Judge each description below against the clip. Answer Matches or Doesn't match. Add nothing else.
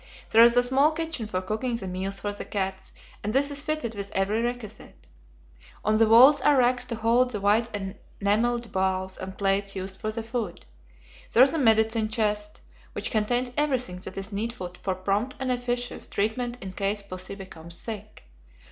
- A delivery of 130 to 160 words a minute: Doesn't match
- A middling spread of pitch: Matches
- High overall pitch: Matches